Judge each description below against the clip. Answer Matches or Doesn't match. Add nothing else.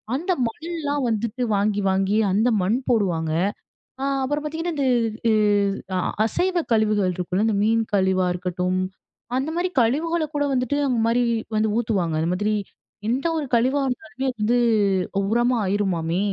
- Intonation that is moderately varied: Doesn't match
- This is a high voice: Matches